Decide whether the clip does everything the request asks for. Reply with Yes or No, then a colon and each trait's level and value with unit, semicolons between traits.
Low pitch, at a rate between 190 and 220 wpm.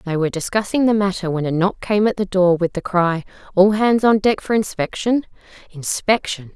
No: high, 195 Hz; average, 200 wpm